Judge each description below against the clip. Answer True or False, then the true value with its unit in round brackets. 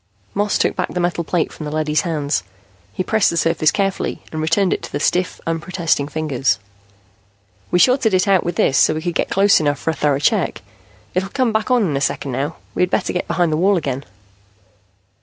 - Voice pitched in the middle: True (165 Hz)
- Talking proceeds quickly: True (215 wpm)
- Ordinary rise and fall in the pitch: True (3.8 semitones)